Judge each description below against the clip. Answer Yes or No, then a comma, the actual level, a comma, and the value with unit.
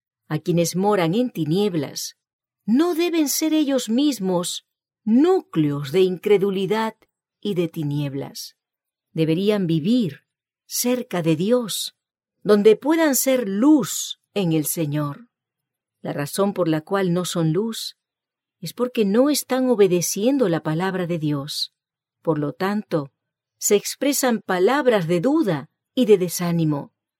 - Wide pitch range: Yes, wide, 7.1 semitones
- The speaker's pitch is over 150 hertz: Yes, high, 190 Hz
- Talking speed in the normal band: No, slow, 125 wpm